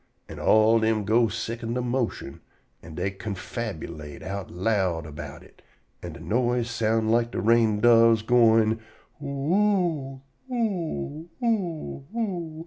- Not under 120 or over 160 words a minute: Yes, slow, 135 wpm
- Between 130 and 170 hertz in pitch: No, low, 115 Hz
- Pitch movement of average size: Yes, average, 4.6 semitones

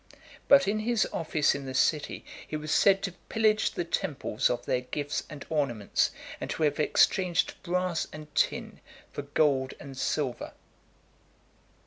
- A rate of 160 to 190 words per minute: No, average, 150 wpm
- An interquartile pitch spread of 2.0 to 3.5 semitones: No, average, 4.5 semitones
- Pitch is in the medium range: Yes, medium, 155 Hz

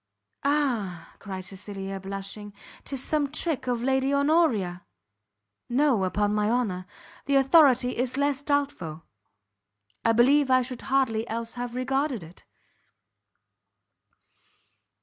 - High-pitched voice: Yes, high, 245 Hz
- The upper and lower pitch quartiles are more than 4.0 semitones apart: Yes, wide, 5.5 semitones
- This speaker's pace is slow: Yes, slow, 110 wpm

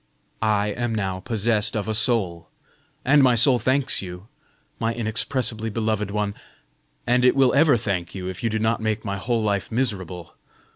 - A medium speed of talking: Yes, average, 175 wpm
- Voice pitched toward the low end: Yes, low, 110 Hz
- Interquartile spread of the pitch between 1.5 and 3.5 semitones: Yes, average, 3.1 semitones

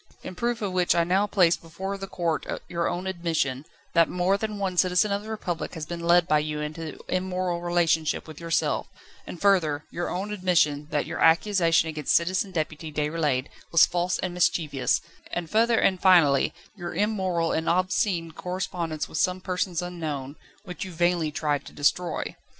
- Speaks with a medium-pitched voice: Yes, medium, 175 Hz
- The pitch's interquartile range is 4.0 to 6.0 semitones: No, narrow, 2.5 semitones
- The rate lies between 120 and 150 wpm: No, average, 175 wpm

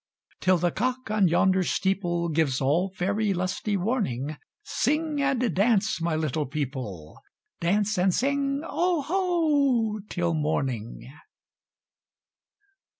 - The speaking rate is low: Yes, slow, 90 wpm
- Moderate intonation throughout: No, wide, 7.7 semitones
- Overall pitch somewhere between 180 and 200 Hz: Yes, high, 190 Hz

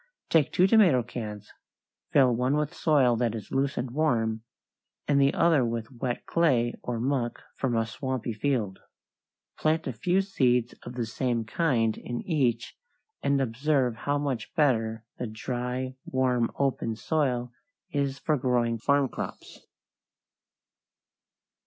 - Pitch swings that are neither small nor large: Yes, average, 3.4 semitones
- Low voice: Yes, low, 125 Hz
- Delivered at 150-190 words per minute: No, average, 140 wpm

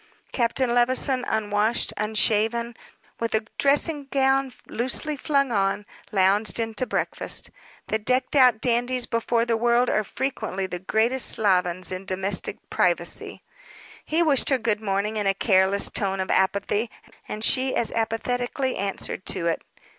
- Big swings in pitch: No, average, 4.0 semitones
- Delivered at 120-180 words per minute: Yes, average, 145 wpm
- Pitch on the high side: Yes, high, 225 Hz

